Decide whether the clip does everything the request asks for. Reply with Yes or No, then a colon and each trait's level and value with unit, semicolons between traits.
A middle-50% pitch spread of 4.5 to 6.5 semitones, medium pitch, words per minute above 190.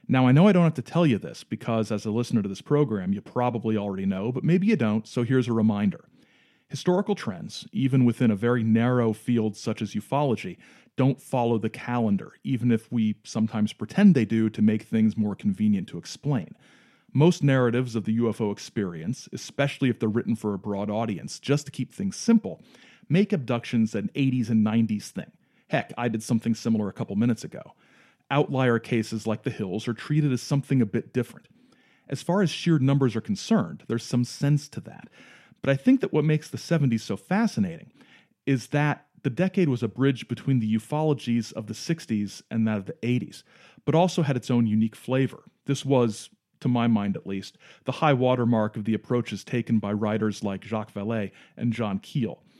No: average, 5.2 semitones; low, 125 Hz; average, 200 wpm